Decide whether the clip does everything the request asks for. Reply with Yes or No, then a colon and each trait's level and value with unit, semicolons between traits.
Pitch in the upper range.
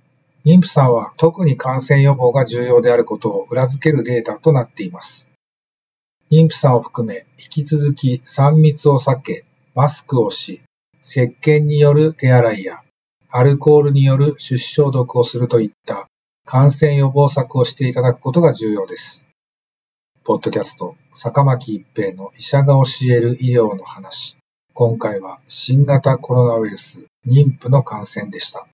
No: low, 135 Hz